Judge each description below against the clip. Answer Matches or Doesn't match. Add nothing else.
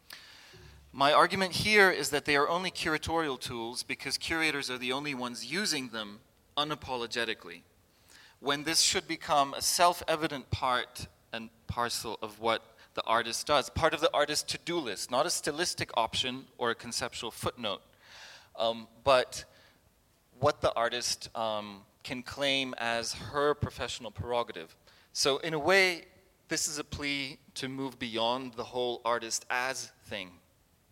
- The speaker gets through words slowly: Doesn't match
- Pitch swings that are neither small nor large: Matches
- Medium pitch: Doesn't match